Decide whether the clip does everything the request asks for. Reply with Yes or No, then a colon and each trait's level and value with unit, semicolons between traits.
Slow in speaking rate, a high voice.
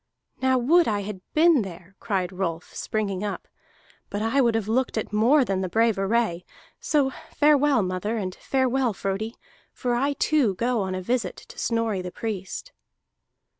No: average, 170 wpm; high, 220 Hz